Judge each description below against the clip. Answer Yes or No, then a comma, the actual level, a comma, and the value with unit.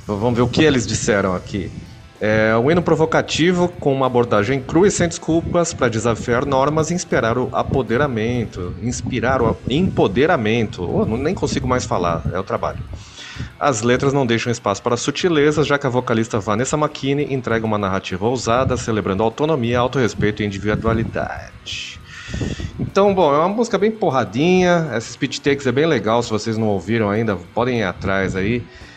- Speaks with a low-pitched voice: Yes, low, 120 Hz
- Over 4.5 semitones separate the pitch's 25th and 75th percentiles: Yes, average, 4.9 semitones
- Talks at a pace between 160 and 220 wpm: Yes, average, 170 wpm